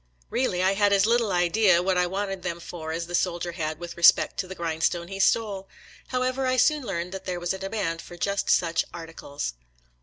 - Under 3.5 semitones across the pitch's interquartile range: Yes, average, 2.8 semitones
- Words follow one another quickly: Yes, fast, 210 wpm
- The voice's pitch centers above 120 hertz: Yes, medium, 185 Hz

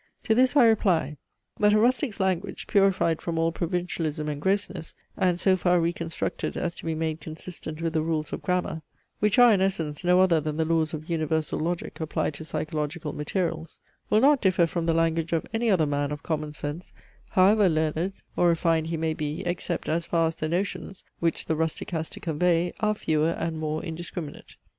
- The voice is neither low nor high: Yes, medium, 165 Hz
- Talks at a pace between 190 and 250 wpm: Yes, average, 195 wpm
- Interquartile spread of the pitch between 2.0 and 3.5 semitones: Yes, average, 2.8 semitones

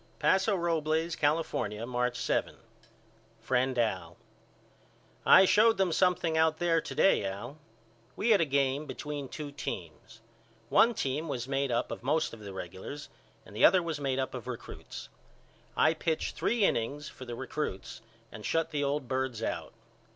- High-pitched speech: No, medium, 140 Hz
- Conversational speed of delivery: Yes, average, 160 wpm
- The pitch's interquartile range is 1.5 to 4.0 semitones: No, average, 4.9 semitones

